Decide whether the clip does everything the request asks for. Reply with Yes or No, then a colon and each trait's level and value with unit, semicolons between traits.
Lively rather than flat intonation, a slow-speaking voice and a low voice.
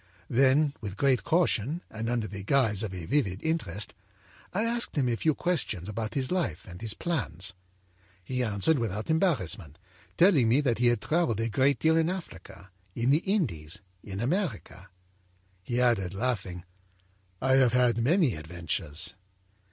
No: wide, 7.0 semitones; average, 160 wpm; low, 120 Hz